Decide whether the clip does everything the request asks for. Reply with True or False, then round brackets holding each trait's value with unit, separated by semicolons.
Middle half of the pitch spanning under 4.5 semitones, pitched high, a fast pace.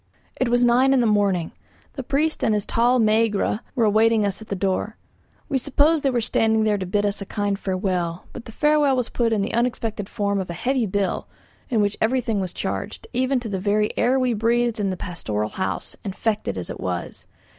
True (3.5 semitones; 220 Hz; 215 wpm)